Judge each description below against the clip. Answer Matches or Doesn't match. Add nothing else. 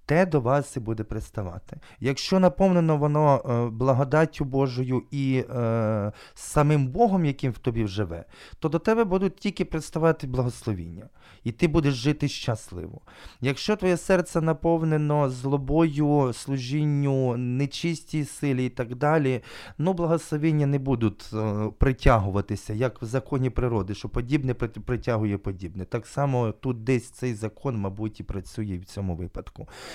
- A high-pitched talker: Doesn't match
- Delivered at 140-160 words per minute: Doesn't match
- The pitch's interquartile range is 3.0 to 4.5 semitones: Doesn't match